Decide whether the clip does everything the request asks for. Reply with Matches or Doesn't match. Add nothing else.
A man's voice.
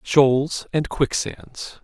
Matches